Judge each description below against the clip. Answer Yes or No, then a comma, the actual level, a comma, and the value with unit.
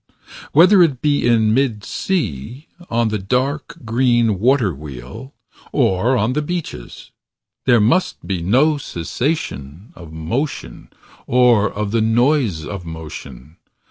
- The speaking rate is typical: No, slow, 125 wpm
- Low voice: Yes, low, 115 Hz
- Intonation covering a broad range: Yes, wide, 7.1 semitones